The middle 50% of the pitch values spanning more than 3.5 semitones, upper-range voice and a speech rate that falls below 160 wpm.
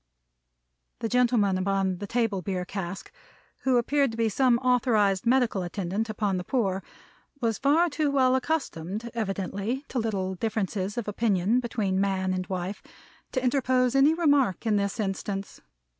Yes: average, 4.6 semitones; high, 215 Hz; average, 150 wpm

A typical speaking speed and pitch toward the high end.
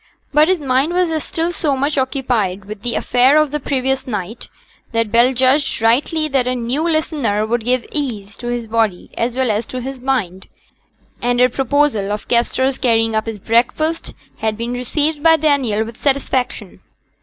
Yes: average, 180 wpm; very high, 250 Hz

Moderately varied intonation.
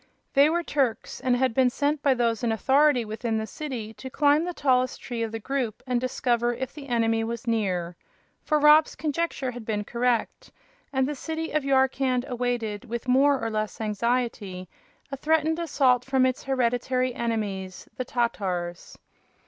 Yes: average, 3.4 semitones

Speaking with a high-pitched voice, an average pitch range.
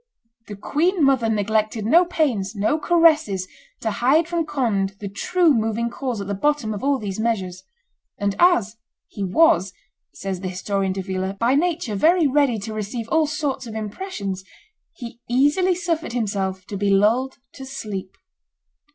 No: high, 225 Hz; wide, 6.8 semitones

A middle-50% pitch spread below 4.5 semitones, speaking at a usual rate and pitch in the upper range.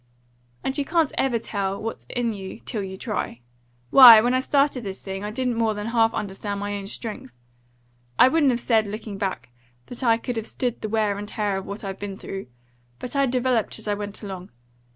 No: average, 3.4 semitones; fast, 215 wpm; high, 215 Hz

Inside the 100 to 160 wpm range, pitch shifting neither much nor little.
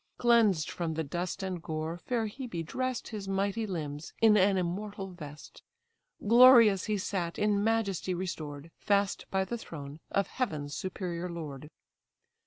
Yes: average, 145 wpm; average, 4.2 semitones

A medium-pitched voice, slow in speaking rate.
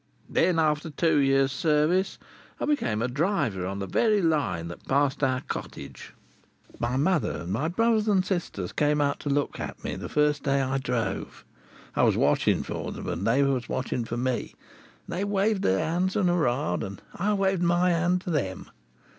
No: medium, 150 Hz; average, 190 wpm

